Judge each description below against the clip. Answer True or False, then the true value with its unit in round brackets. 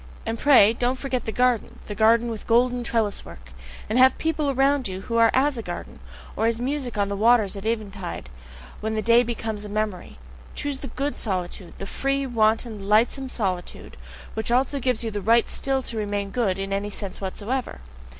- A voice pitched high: True (225 Hz)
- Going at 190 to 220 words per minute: True (200 wpm)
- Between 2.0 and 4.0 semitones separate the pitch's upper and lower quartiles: True (3.6 semitones)